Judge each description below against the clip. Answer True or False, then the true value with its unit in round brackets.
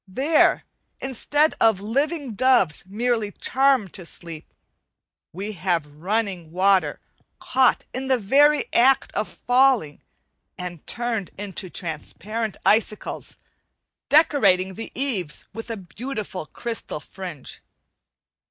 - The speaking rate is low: True (105 wpm)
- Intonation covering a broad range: True (5.8 semitones)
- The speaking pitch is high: True (215 Hz)